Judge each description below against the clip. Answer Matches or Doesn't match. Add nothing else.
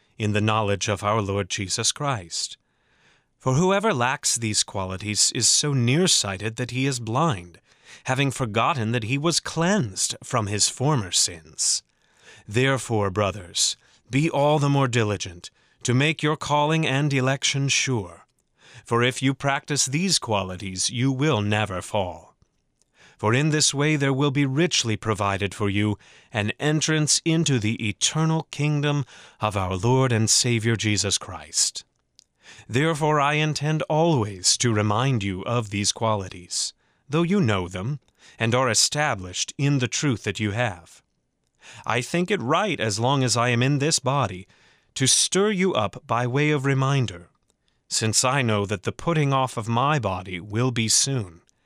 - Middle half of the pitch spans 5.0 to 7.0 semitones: Matches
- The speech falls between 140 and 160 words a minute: Matches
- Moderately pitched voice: Doesn't match